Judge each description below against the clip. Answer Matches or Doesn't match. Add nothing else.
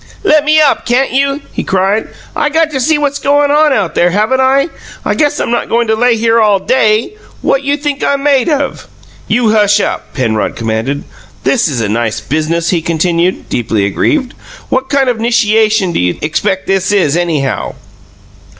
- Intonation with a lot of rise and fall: Matches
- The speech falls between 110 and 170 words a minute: Doesn't match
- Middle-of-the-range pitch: Doesn't match